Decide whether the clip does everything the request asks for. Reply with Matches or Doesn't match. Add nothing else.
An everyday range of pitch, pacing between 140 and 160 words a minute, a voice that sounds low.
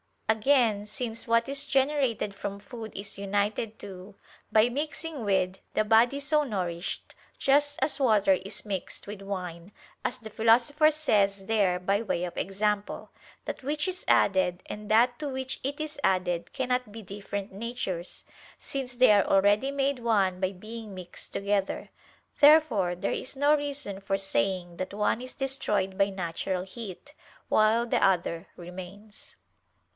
Doesn't match